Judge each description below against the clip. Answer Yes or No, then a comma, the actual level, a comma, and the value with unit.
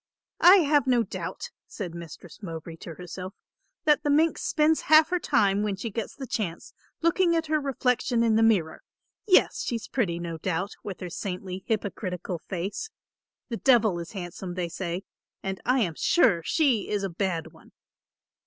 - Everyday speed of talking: Yes, average, 170 wpm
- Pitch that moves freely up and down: Yes, wide, 7.0 semitones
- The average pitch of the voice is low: No, high, 205 Hz